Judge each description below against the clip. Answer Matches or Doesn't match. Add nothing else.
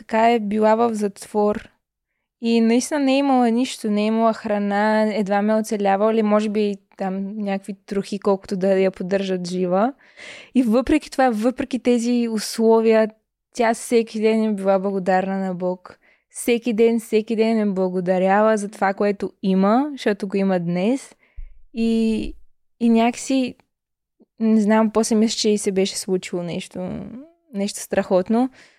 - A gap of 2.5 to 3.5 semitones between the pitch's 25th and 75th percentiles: Matches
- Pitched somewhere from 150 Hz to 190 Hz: Doesn't match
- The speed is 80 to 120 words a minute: Doesn't match